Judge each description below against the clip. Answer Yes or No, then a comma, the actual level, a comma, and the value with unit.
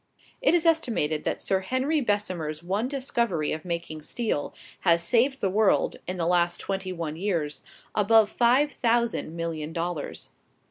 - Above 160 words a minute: No, average, 150 wpm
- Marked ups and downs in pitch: Yes, wide, 6.0 semitones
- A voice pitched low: No, high, 190 Hz